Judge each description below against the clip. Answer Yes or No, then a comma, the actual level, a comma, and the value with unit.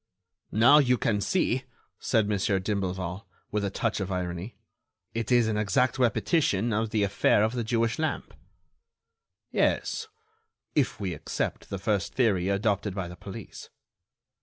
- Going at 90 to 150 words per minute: Yes, average, 145 wpm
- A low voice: Yes, low, 105 Hz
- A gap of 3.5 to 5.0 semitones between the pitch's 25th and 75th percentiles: No, average, 3.1 semitones